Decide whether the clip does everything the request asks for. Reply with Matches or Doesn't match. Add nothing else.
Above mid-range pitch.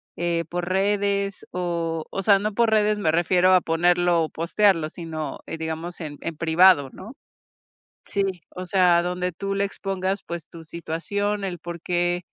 Doesn't match